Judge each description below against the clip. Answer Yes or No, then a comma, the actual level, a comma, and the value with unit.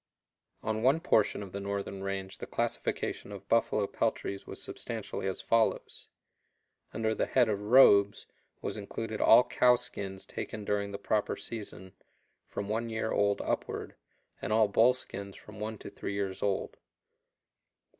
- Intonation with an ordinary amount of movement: No, narrow, 1.9 semitones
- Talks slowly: No, average, 155 wpm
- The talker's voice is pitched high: No, low, 105 Hz